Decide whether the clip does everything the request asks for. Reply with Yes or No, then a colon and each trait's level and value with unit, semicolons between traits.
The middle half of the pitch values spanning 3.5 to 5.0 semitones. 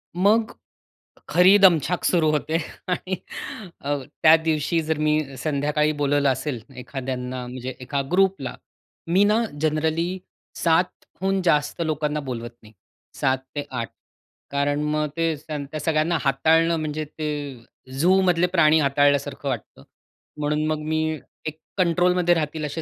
No: average, 2.9 semitones